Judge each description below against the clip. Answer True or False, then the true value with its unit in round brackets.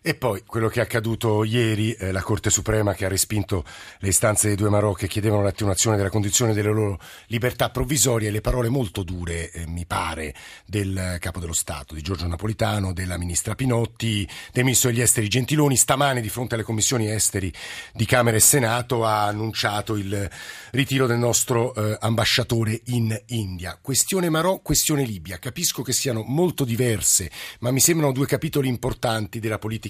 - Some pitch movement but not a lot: True (3.6 semitones)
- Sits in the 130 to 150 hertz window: False (110 Hz)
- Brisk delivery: True (175 wpm)